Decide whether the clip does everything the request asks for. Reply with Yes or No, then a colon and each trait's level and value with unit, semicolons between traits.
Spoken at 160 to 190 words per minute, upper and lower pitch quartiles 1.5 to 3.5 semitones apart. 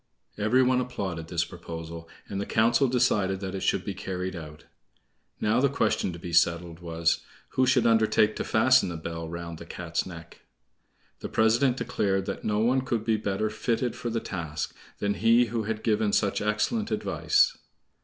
No: average, 180 wpm; average, 5.3 semitones